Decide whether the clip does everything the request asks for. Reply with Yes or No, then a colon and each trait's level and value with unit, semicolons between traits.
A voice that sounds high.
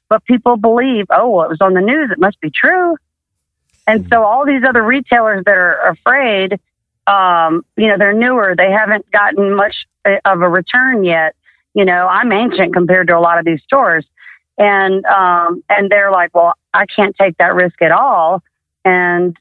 Yes: high, 195 Hz